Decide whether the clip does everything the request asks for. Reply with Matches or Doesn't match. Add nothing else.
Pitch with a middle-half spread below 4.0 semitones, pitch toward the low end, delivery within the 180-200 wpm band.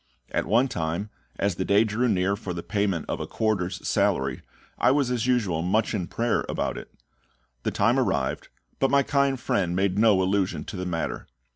Doesn't match